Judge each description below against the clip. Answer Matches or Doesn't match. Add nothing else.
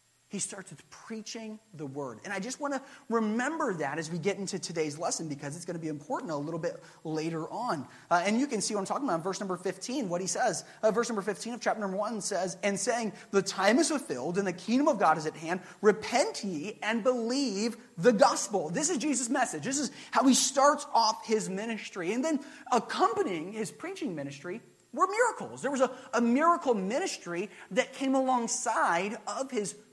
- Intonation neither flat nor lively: Doesn't match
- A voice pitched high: Matches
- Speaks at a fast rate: Matches